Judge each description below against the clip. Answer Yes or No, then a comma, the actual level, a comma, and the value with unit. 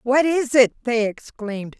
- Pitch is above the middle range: Yes, high, 245 Hz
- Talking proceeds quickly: No, average, 165 wpm